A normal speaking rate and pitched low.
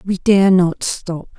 No: average, 175 wpm; medium, 185 Hz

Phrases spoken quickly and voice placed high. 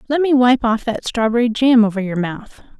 Yes: fast, 215 wpm; high, 235 Hz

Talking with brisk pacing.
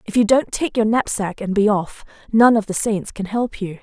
Yes: fast, 250 wpm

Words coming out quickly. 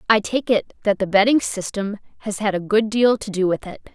Yes: fast, 245 wpm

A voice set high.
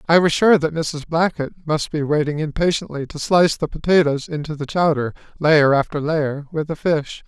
No: medium, 155 Hz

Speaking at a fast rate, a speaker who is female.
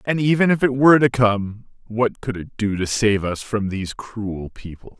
No: fast, 215 wpm; male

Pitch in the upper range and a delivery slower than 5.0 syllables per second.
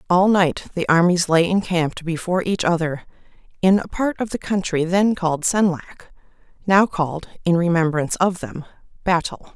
No: medium, 175 Hz; 4.6 syllables/s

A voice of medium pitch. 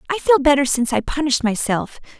No: very high, 275 Hz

